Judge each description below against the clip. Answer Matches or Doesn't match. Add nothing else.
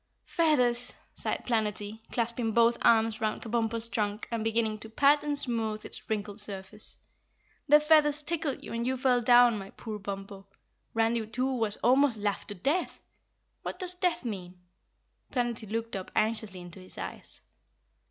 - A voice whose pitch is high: Matches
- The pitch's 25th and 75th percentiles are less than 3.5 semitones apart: Matches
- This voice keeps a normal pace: Matches